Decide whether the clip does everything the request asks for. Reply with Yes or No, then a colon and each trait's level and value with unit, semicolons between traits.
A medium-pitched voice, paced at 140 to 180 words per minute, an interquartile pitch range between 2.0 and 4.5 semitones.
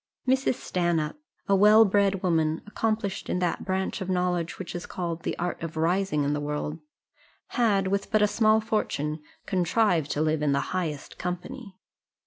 Yes: medium, 180 Hz; average, 170 wpm; average, 4.1 semitones